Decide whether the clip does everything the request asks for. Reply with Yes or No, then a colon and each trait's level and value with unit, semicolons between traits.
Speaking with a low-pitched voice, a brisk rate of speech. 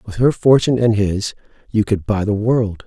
No: low, 110 Hz; average, 190 wpm